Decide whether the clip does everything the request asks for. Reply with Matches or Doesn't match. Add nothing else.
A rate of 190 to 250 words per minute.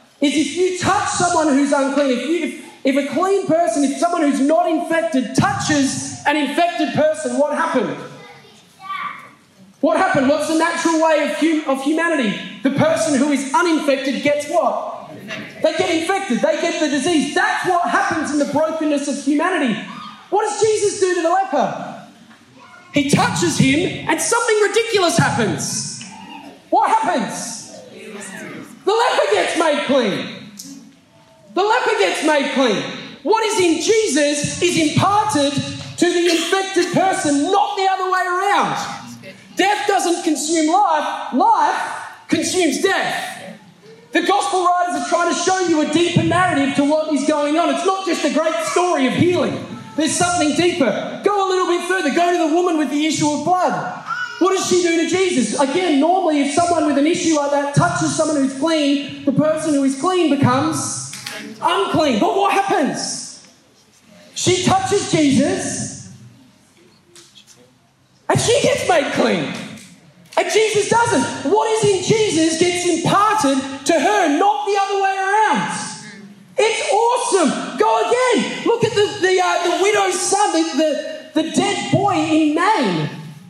Doesn't match